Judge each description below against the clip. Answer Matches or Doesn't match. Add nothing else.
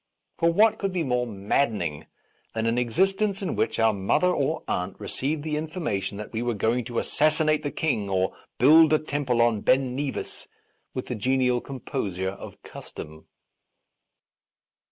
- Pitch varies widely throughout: Matches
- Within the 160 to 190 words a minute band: Matches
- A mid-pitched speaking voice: Doesn't match